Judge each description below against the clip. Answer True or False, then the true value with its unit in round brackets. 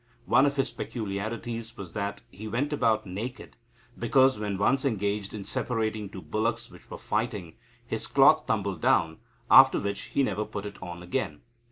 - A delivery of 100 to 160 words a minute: False (170 wpm)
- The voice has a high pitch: False (110 Hz)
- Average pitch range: True (3.2 semitones)